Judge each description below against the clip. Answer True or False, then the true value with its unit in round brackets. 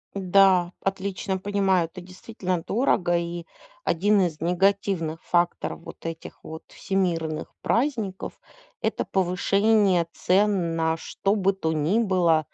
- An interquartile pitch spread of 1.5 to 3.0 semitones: True (2.7 semitones)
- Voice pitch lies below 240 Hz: True (185 Hz)